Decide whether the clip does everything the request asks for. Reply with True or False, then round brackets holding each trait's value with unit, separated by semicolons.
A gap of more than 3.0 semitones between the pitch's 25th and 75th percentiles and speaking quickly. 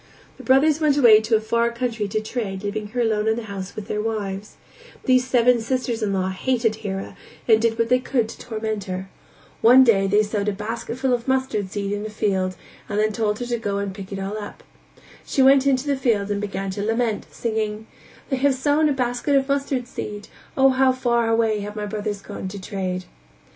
True (3.5 semitones; 215 wpm)